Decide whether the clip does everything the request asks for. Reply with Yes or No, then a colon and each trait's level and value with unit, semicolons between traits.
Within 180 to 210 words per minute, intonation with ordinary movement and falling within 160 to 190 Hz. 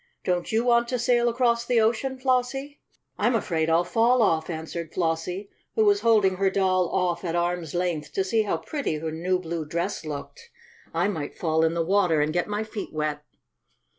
No: average, 195 wpm; wide, 6.1 semitones; medium, 185 Hz